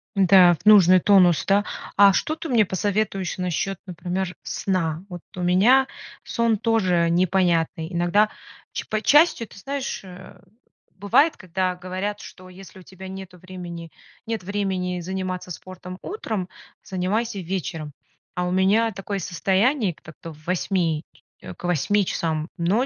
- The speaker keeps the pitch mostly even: Yes, narrow, 2.3 semitones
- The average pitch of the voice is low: No, medium, 185 Hz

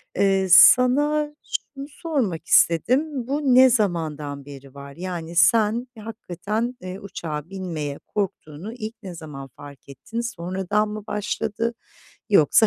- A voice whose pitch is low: No, high, 195 Hz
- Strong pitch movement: Yes, wide, 6.3 semitones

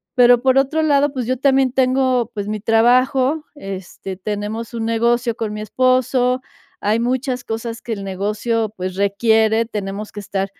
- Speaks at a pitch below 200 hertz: No, high, 230 Hz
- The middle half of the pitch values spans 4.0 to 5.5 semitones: No, average, 3.3 semitones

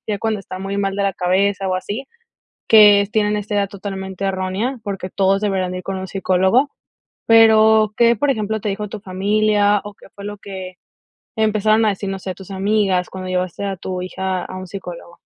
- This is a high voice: Yes, high, 200 Hz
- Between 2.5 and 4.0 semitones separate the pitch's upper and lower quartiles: No, narrow, 2.1 semitones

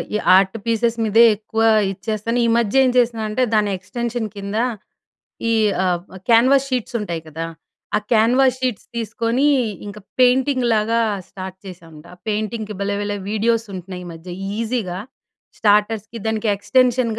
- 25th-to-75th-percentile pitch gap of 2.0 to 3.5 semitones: Yes, average, 2.8 semitones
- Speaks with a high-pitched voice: Yes, high, 220 Hz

